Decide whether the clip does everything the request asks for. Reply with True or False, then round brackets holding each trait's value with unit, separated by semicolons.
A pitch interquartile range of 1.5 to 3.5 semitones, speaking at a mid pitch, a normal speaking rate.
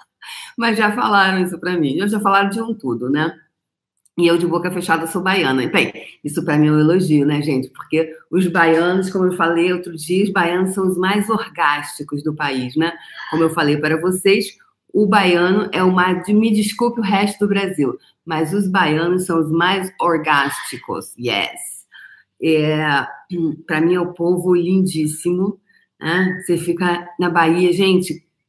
True (2.9 semitones; 175 Hz; 175 wpm)